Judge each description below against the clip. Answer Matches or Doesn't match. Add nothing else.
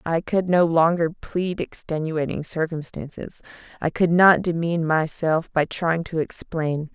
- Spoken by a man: Doesn't match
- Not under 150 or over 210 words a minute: Doesn't match